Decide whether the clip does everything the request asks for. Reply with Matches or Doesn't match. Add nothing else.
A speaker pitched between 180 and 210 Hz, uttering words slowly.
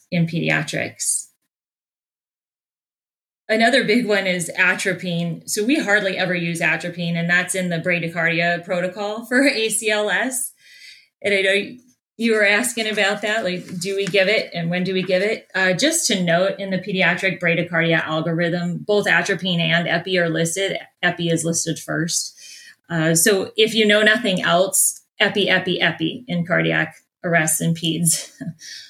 Doesn't match